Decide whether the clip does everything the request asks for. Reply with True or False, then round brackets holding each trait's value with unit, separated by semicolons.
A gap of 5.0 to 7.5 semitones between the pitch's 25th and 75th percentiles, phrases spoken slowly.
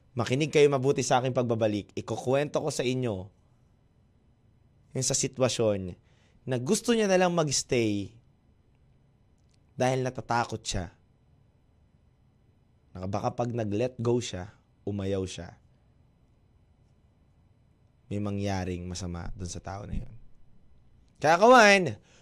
False (4.2 semitones; 105 wpm)